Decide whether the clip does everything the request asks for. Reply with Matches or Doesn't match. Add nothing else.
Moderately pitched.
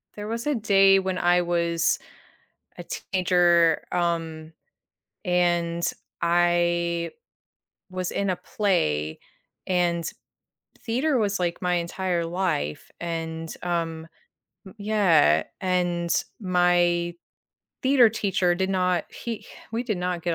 Matches